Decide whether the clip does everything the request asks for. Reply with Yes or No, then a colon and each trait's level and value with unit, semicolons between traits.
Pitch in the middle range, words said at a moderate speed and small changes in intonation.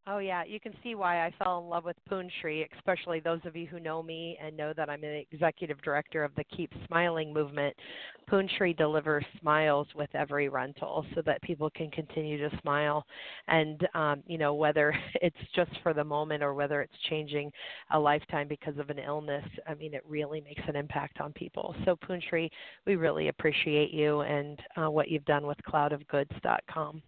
Yes: medium, 155 Hz; average, 190 wpm; narrow, 2.3 semitones